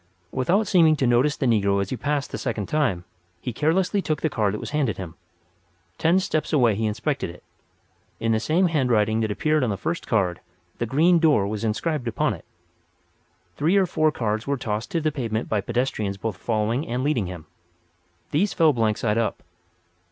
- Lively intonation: Yes, wide, 6.2 semitones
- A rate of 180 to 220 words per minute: Yes, average, 195 wpm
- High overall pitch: No, low, 120 Hz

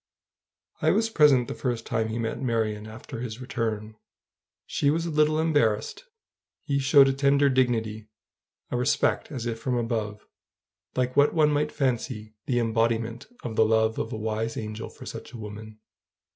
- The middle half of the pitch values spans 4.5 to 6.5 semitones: No, average, 3.7 semitones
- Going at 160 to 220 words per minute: Yes, average, 170 wpm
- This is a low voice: Yes, low, 115 Hz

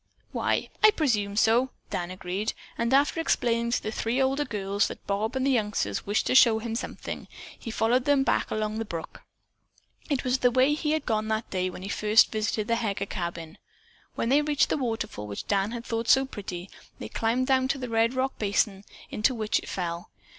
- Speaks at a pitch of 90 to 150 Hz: No, high, 225 Hz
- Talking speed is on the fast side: Yes, fast, 215 wpm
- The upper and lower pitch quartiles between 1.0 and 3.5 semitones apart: No, average, 4.1 semitones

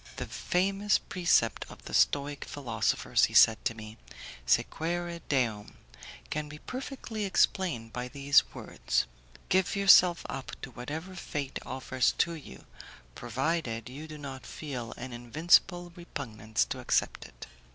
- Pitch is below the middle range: No, medium, 145 Hz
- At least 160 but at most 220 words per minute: No, slow, 135 wpm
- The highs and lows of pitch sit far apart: Yes, wide, 6.4 semitones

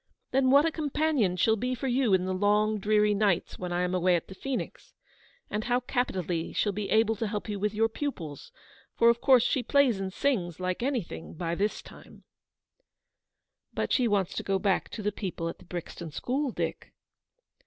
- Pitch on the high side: Yes, high, 210 Hz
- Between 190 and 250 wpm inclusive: Yes, average, 200 wpm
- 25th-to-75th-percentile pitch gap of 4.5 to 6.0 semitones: Yes, average, 5.1 semitones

